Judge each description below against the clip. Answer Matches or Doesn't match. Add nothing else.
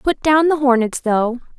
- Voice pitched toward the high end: Matches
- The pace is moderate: Matches